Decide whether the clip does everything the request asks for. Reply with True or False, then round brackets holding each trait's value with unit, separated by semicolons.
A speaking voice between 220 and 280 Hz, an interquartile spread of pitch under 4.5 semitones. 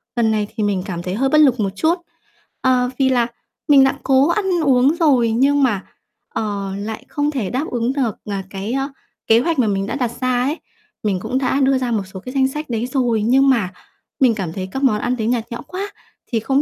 True (250 Hz; 3.9 semitones)